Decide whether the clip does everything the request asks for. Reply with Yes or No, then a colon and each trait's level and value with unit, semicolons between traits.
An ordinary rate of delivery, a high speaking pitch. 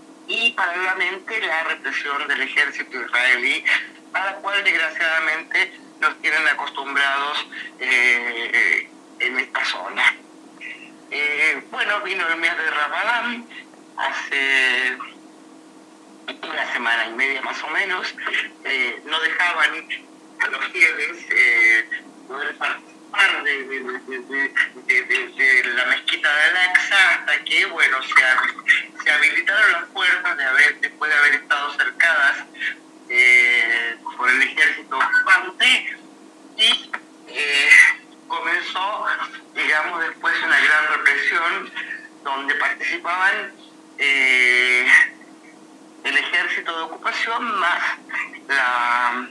No: slow, 105 wpm; very high, 315 Hz